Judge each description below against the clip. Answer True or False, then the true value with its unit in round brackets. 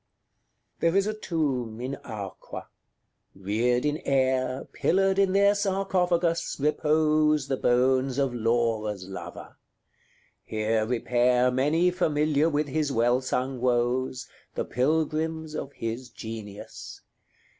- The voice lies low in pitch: True (130 Hz)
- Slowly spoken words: True (115 wpm)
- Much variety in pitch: False (4.6 semitones)